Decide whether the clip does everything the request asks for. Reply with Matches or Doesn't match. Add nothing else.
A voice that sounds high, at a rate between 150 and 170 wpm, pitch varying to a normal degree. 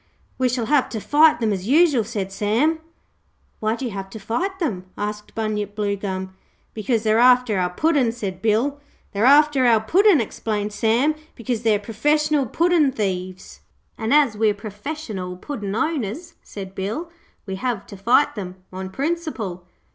Doesn't match